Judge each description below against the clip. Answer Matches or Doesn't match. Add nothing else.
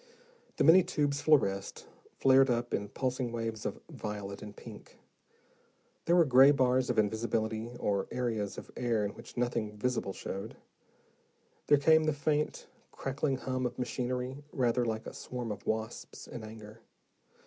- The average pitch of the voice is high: Doesn't match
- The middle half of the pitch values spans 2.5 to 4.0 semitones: Matches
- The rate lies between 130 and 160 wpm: Matches